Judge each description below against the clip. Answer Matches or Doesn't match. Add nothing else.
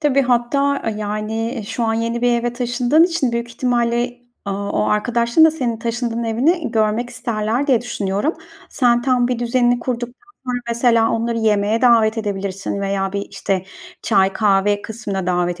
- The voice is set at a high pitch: Matches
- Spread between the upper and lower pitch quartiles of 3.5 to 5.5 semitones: Doesn't match